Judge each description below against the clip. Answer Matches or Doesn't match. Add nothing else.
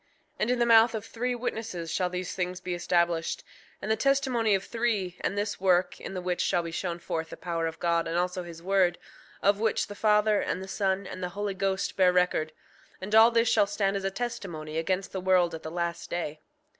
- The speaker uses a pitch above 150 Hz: Matches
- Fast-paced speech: Matches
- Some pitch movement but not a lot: Matches